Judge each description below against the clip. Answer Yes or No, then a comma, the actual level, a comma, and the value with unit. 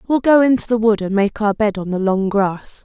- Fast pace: Yes, fast, 275 wpm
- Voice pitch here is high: Yes, high, 215 Hz